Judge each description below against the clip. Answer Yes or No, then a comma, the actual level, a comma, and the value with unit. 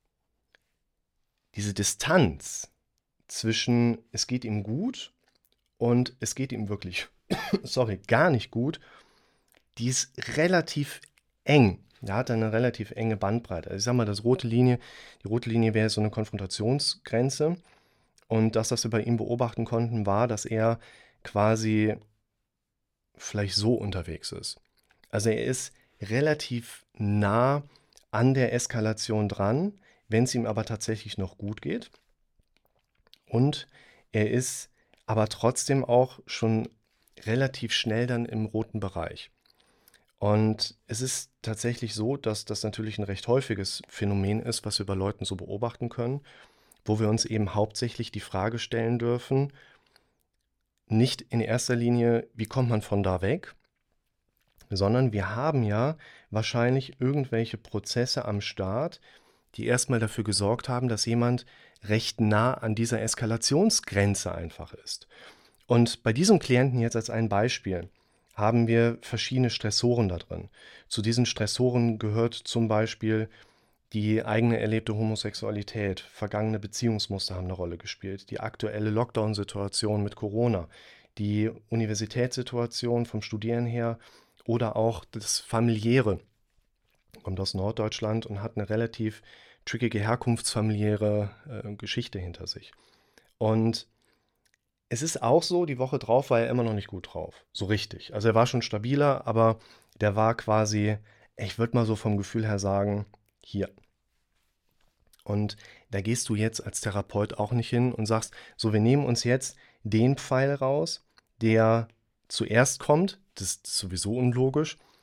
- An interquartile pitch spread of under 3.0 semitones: Yes, narrow, 2.4 semitones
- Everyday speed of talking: Yes, average, 140 wpm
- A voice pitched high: No, low, 115 Hz